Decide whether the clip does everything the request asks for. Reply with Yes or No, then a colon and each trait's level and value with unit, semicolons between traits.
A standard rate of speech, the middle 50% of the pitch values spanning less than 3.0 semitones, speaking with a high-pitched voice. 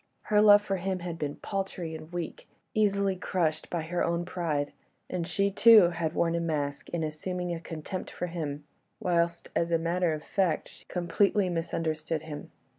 No: average, 180 wpm; narrow, 2.4 semitones; medium, 170 Hz